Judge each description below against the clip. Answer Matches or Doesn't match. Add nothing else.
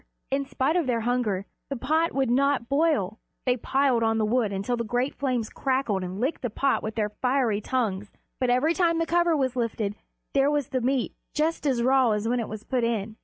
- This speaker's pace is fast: Matches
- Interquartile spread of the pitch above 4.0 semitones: Doesn't match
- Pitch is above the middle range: Matches